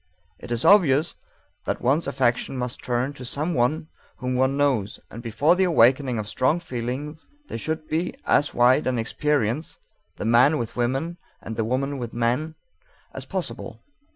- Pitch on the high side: No, low, 130 Hz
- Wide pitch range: No, average, 4.0 semitones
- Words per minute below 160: No, average, 165 wpm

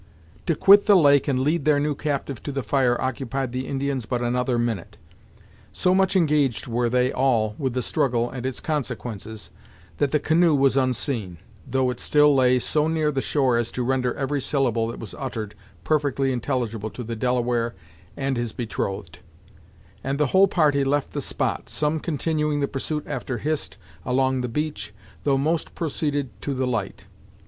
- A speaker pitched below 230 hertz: Yes, low, 135 Hz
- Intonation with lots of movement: No, average, 3.3 semitones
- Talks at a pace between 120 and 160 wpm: No, average, 175 wpm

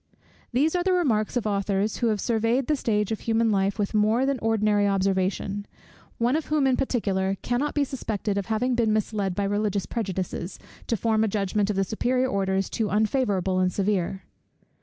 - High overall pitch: Yes, high, 215 Hz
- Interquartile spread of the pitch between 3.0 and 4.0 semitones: Yes, average, 3.3 semitones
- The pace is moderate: Yes, average, 185 wpm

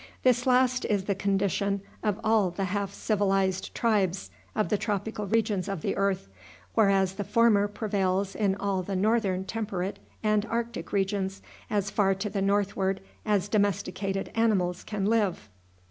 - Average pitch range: No, narrow, 1.8 semitones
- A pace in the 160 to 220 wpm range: No, average, 150 wpm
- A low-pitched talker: No, high, 200 Hz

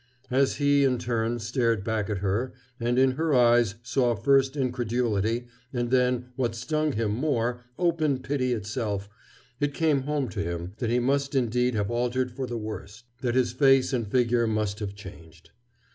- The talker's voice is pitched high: No, low, 120 Hz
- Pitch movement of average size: Yes, average, 3.0 semitones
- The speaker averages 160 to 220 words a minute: Yes, average, 175 wpm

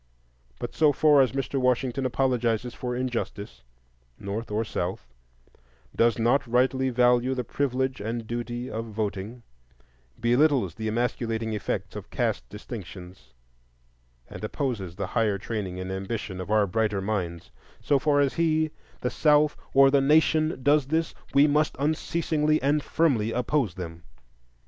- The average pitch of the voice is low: Yes, low, 120 Hz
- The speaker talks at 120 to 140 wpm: Yes, slow, 135 wpm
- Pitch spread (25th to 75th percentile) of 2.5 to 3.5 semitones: No, average, 4.7 semitones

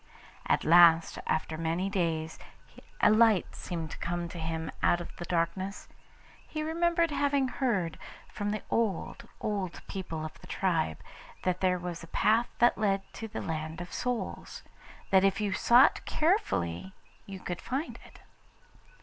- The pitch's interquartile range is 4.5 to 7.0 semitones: Yes, average, 5.1 semitones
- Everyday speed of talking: Yes, average, 155 wpm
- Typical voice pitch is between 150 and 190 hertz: Yes, medium, 185 Hz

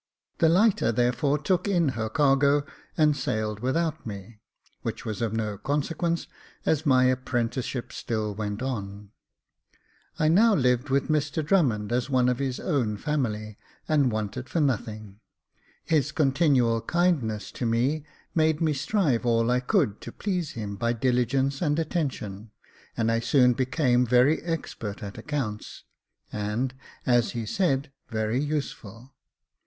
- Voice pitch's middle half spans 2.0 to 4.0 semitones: No, average, 4.9 semitones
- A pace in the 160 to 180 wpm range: No, average, 140 wpm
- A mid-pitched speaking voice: No, low, 130 Hz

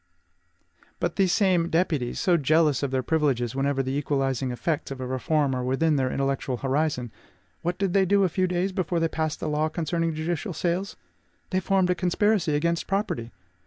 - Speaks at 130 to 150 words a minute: No, average, 185 wpm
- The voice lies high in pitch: No, medium, 160 Hz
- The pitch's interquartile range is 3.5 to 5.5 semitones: Yes, average, 4.7 semitones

